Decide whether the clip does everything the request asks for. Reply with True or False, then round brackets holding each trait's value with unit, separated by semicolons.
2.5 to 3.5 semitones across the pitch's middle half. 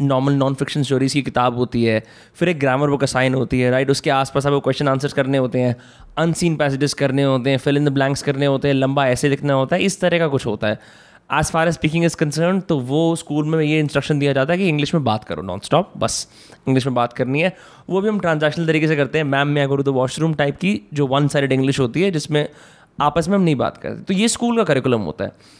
True (3.2 semitones)